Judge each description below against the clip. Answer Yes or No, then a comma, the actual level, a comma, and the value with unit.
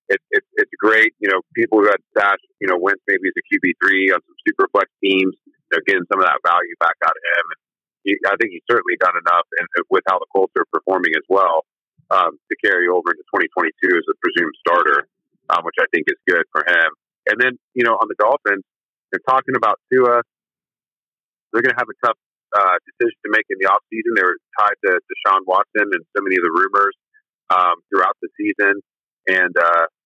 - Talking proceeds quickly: Yes, fast, 220 wpm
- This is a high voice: Yes, very high, 370 Hz